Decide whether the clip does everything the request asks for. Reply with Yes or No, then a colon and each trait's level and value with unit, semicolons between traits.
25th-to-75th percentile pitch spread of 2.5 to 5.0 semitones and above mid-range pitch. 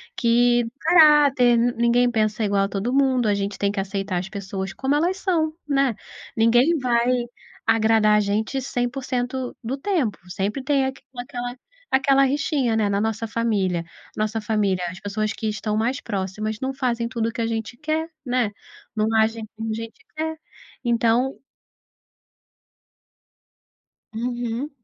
Yes: average, 3.5 semitones; high, 235 Hz